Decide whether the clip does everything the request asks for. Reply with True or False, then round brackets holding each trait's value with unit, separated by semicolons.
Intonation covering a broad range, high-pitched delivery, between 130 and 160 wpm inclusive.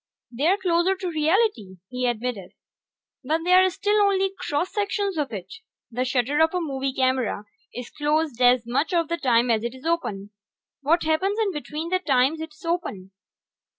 False (6.2 semitones; 305 Hz; 175 wpm)